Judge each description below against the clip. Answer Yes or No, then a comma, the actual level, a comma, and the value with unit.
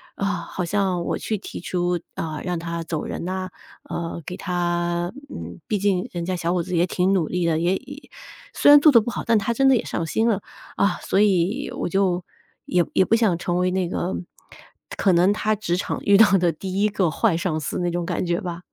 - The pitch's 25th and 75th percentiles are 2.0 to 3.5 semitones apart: Yes, narrow, 2.5 semitones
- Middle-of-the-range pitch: Yes, medium, 180 Hz